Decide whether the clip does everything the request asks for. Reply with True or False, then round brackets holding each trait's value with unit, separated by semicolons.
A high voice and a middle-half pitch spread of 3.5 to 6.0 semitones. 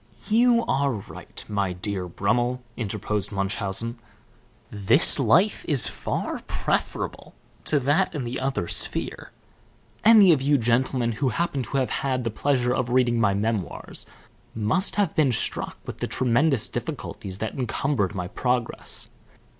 False (125 Hz; 4.8 semitones)